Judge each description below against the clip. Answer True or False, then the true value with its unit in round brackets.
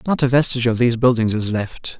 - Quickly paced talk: True (240 wpm)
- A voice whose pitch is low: True (120 Hz)